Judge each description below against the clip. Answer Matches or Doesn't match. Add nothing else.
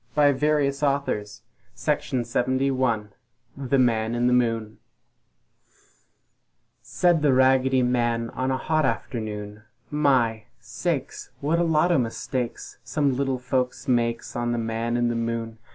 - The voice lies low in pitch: Matches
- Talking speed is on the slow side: Matches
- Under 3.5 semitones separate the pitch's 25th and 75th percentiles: Matches